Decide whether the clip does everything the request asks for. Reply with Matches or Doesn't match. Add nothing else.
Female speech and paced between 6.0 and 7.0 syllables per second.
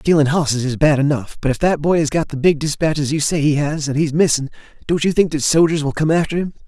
Doesn't match